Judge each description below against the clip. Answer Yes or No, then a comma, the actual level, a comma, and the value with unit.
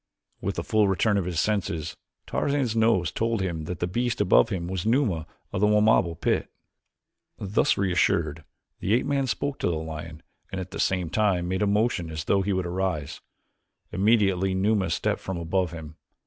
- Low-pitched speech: Yes, very low, 95 Hz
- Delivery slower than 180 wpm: No, average, 185 wpm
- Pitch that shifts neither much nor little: Yes, average, 3.8 semitones